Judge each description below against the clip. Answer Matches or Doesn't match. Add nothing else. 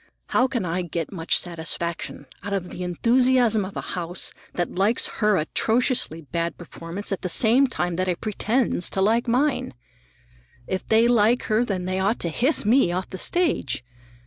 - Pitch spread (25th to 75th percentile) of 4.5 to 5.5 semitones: Matches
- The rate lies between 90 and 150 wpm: Doesn't match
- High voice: Matches